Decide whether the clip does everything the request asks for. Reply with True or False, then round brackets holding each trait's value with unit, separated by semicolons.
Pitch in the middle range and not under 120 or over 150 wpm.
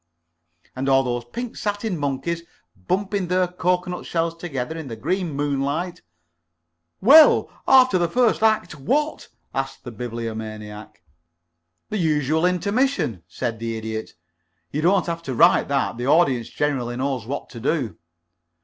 True (145 Hz; 140 wpm)